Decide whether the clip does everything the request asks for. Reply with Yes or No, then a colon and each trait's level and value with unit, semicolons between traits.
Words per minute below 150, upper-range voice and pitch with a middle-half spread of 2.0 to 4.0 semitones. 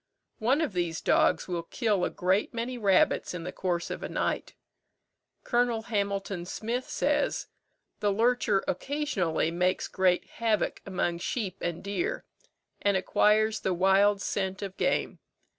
Yes: average, 140 wpm; high, 200 Hz; average, 3.6 semitones